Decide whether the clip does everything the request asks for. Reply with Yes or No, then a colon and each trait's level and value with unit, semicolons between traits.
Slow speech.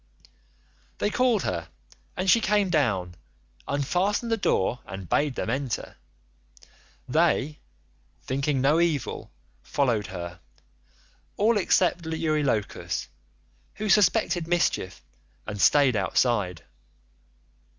Yes: slow, 100 wpm